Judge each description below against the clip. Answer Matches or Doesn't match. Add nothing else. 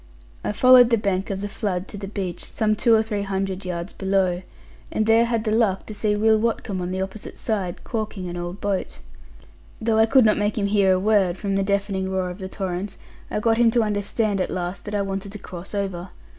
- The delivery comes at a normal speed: Doesn't match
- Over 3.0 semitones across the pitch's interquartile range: Doesn't match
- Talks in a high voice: Matches